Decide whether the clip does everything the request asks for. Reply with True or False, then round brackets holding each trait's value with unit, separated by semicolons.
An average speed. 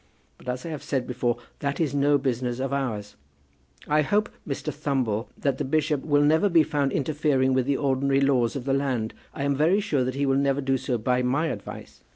False (215 wpm)